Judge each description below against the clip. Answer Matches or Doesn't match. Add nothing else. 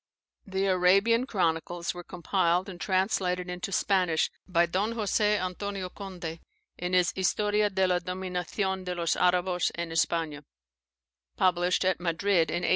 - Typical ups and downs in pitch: Doesn't match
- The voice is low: Doesn't match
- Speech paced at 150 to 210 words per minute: Doesn't match